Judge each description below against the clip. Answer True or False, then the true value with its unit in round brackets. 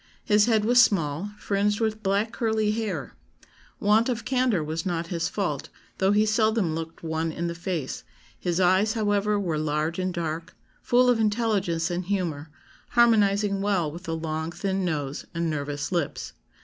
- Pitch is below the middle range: False (190 Hz)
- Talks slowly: False (165 wpm)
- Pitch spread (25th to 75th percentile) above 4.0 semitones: True (4.4 semitones)